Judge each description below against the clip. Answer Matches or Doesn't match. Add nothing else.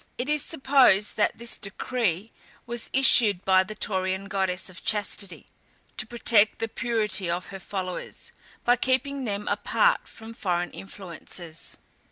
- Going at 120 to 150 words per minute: Matches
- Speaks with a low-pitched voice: Doesn't match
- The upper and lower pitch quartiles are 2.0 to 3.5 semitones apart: Doesn't match